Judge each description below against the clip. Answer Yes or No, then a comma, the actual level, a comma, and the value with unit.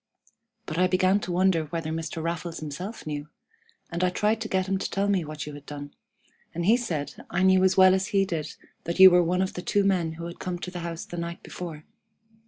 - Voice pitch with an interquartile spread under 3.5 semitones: Yes, narrow, 2.6 semitones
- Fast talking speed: Yes, fast, 240 wpm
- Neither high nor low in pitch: Yes, medium, 175 Hz